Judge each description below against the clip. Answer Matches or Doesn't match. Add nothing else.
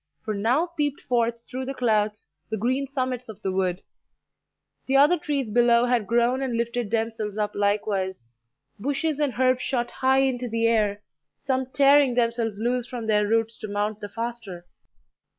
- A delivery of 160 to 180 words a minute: Matches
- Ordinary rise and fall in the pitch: Matches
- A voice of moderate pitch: Doesn't match